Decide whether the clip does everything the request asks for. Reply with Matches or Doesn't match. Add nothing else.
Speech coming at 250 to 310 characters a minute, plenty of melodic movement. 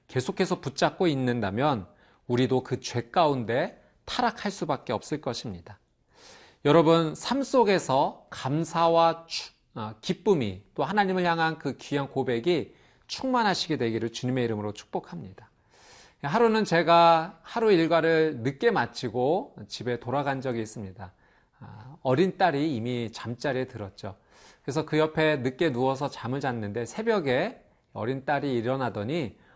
Matches